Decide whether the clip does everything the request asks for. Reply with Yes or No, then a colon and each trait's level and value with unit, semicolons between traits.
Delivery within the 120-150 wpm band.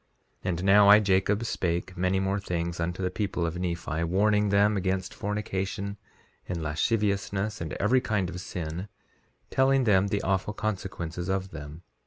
No: average, 160 wpm